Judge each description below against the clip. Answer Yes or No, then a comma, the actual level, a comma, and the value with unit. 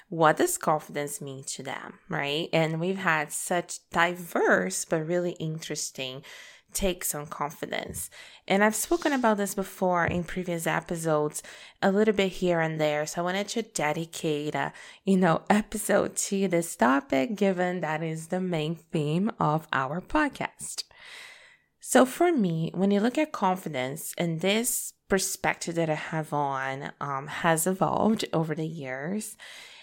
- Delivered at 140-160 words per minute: Yes, average, 150 wpm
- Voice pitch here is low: No, medium, 175 Hz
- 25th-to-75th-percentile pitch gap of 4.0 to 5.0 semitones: Yes, average, 4.5 semitones